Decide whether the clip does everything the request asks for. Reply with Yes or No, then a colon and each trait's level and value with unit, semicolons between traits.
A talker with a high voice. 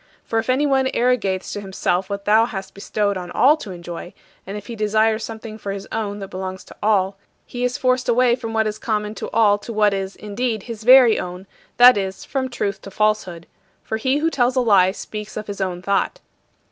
Yes: high, 215 Hz